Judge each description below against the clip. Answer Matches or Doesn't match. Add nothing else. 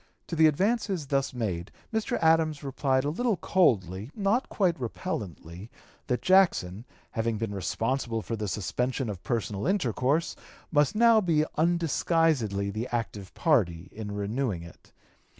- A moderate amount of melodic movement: Doesn't match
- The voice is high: Doesn't match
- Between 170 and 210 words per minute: Doesn't match